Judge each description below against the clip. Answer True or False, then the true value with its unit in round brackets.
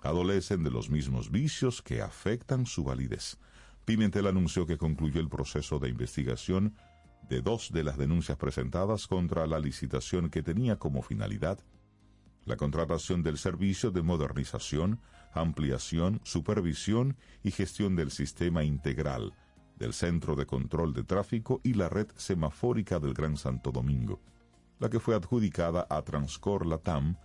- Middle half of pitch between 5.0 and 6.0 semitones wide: True (5.3 semitones)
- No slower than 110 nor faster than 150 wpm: True (140 wpm)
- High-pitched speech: False (85 Hz)